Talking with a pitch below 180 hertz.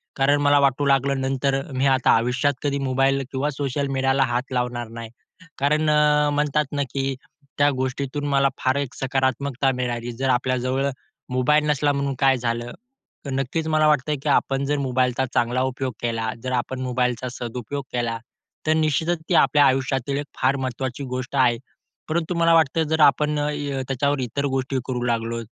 Yes: low, 135 Hz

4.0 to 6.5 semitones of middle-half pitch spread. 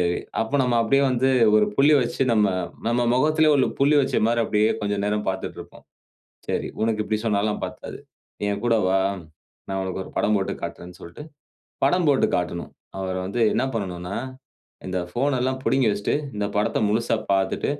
Yes: average, 4.7 semitones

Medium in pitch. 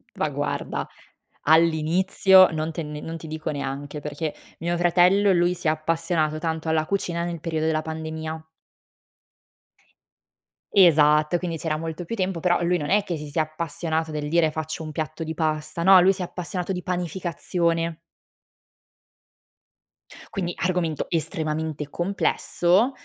Yes: medium, 165 Hz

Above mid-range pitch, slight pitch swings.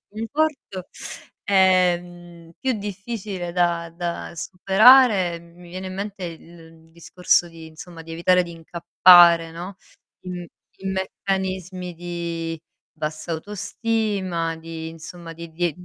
No: medium, 175 Hz; narrow, 2.3 semitones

